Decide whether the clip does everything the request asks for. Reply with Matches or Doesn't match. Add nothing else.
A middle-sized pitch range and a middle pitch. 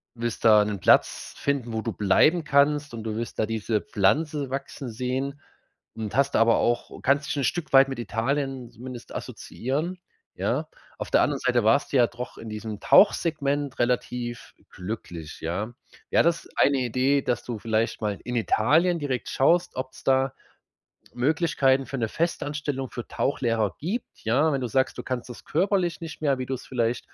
Doesn't match